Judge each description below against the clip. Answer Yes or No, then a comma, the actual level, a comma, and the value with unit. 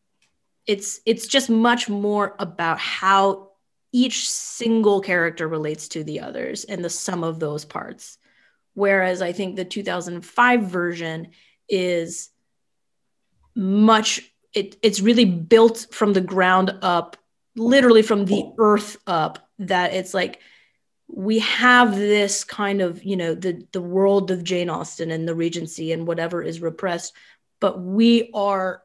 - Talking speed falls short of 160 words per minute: Yes, average, 140 wpm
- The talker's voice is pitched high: Yes, high, 195 Hz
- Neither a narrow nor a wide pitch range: Yes, average, 3.4 semitones